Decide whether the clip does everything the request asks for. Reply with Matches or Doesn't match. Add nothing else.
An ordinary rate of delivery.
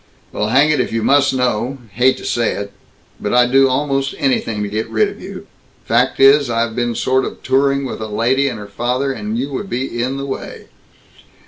Doesn't match